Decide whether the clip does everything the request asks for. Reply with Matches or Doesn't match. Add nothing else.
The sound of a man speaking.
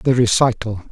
Matches